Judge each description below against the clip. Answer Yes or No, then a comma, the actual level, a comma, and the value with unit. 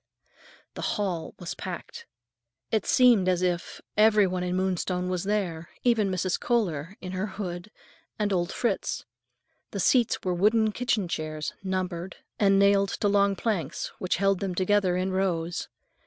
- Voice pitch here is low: No, high, 190 Hz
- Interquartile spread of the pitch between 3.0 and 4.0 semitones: No, narrow, 2.4 semitones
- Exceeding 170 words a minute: No, average, 155 wpm